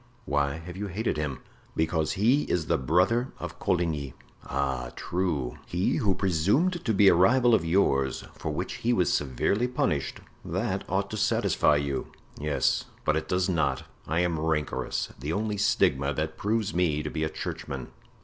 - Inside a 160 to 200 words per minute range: Yes, average, 170 wpm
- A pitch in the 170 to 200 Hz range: No, very low, 85 Hz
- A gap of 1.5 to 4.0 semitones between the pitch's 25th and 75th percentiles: No, average, 5.2 semitones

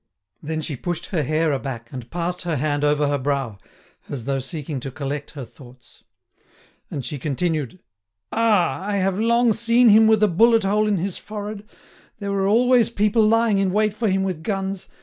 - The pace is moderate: Yes, average, 190 wpm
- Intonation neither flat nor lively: No, wide, 6.5 semitones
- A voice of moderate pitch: Yes, medium, 180 Hz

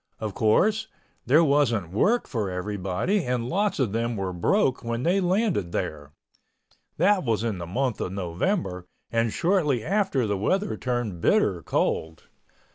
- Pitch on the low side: Yes, low, 115 Hz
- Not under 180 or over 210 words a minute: No, average, 145 wpm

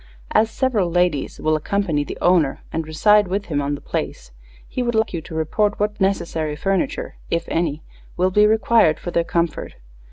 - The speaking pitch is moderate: Yes, medium, 175 Hz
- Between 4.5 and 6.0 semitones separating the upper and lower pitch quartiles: Yes, average, 4.8 semitones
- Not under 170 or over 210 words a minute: Yes, average, 185 wpm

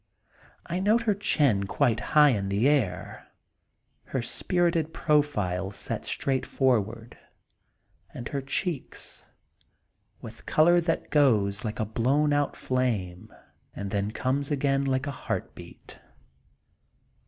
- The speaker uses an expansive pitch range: Yes, wide, 5.8 semitones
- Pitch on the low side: Yes, low, 130 Hz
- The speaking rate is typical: No, slow, 125 wpm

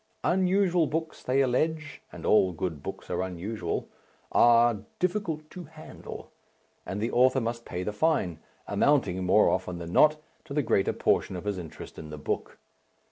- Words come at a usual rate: Yes, average, 165 wpm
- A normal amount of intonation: No, wide, 8.9 semitones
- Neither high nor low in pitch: No, low, 120 Hz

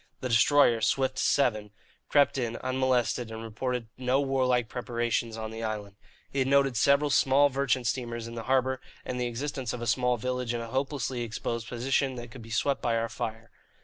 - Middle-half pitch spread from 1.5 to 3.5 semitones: Yes, narrow, 2.4 semitones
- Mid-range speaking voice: No, low, 125 Hz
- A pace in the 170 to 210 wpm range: Yes, average, 185 wpm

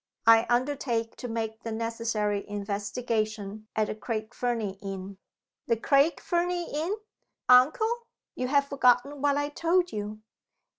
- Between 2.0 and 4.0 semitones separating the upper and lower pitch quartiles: No, average, 4.8 semitones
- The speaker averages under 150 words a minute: Yes, slow, 135 wpm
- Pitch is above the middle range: Yes, high, 230 Hz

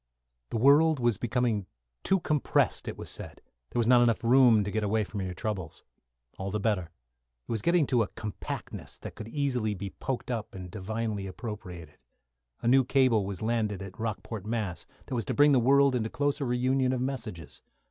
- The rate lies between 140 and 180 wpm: No, average, 190 wpm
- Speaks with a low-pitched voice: Yes, low, 115 Hz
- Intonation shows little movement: No, average, 3.7 semitones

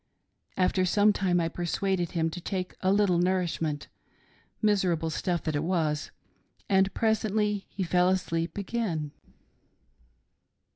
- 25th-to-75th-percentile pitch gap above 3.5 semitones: No, average, 2.9 semitones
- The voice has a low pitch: No, medium, 180 Hz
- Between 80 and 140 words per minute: Yes, slow, 135 wpm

